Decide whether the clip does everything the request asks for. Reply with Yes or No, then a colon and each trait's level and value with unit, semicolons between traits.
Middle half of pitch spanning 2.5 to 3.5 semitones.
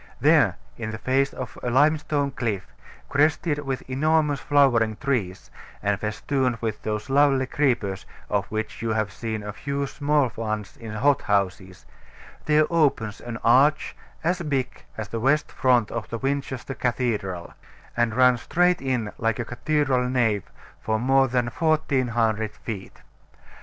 No: average, 4.4 semitones